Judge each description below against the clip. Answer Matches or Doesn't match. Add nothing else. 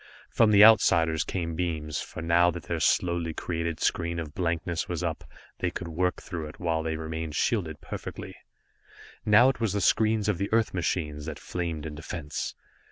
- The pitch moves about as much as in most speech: Doesn't match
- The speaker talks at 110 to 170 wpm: Doesn't match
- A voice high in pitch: Doesn't match